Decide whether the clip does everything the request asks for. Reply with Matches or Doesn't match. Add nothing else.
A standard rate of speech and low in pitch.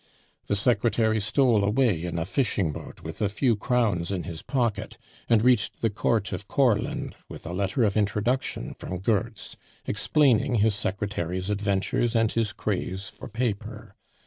Matches